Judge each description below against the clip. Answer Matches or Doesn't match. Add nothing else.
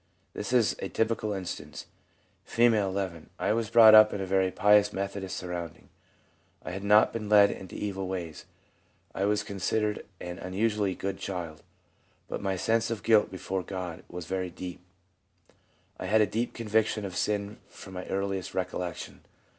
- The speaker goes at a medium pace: Matches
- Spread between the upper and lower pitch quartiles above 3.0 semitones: Doesn't match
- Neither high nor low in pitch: Doesn't match